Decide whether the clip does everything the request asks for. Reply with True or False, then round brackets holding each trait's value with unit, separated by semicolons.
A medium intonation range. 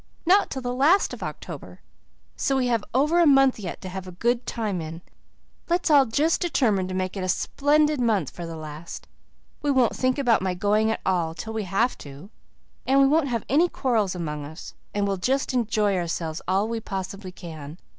False (6.6 semitones)